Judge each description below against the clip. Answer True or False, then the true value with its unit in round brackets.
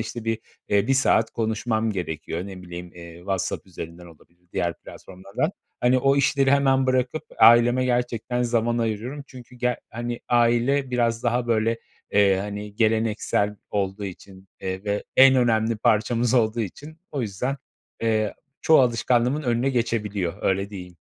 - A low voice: True (115 Hz)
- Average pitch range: True (3.7 semitones)